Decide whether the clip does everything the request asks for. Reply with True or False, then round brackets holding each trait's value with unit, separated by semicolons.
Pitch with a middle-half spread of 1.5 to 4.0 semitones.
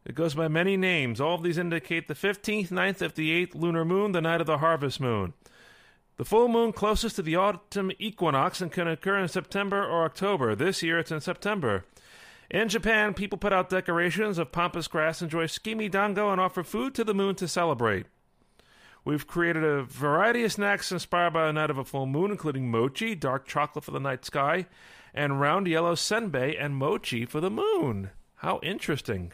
False (4.7 semitones)